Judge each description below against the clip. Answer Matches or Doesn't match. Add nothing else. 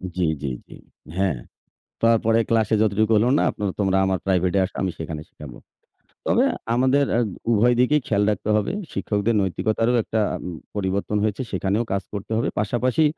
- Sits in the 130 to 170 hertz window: Doesn't match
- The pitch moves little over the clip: Doesn't match